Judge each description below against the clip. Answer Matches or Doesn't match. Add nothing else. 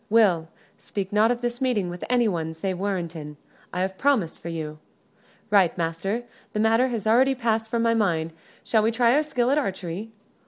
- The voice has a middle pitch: Doesn't match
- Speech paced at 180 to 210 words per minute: Matches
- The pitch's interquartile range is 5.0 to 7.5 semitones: Matches